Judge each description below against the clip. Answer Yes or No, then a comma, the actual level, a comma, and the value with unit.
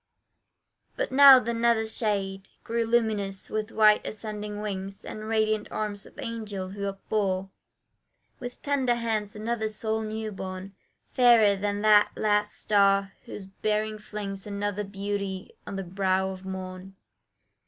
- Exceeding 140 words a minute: No, slow, 135 wpm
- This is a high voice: Yes, high, 210 Hz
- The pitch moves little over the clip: Yes, narrow, 2.0 semitones